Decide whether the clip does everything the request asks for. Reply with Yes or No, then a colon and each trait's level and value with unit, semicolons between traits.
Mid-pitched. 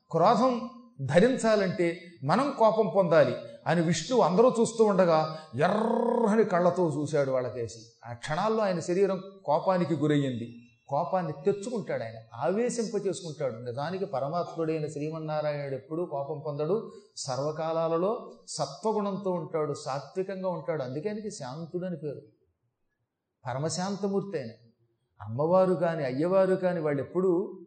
Yes: medium, 170 Hz